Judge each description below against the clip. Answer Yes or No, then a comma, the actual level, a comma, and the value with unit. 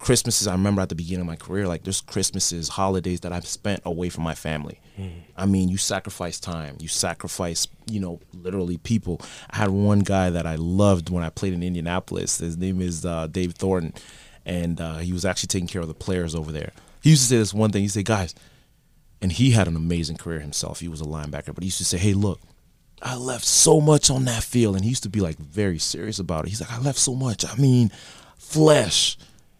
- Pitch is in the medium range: No, very low, 95 Hz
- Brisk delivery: Yes, fast, 235 wpm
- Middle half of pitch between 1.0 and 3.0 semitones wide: No, average, 3.5 semitones